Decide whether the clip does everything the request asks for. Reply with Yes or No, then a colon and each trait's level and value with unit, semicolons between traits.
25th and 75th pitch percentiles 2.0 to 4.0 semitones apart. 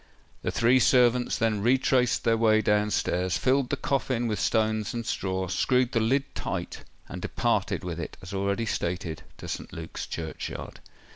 No: average, 4.5 semitones